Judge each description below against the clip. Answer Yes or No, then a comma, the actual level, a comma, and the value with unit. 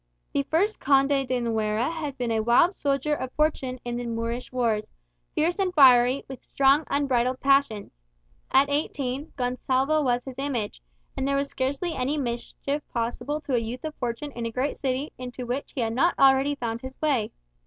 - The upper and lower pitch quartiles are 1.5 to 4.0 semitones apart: Yes, average, 2.8 semitones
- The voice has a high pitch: Yes, very high, 265 Hz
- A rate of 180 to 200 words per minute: Yes, average, 185 wpm